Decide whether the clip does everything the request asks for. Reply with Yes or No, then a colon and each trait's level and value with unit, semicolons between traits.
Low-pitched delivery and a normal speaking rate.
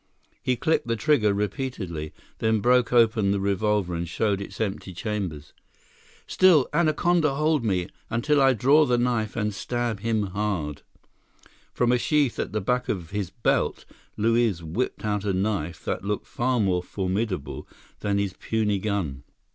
Yes: low, 105 Hz; average, 155 wpm